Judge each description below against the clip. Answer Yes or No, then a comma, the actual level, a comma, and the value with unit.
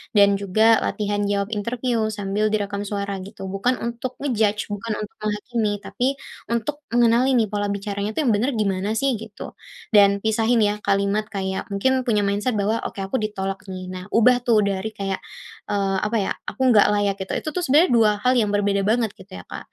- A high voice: Yes, high, 210 Hz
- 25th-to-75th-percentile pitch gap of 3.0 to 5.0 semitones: No, narrow, 2.6 semitones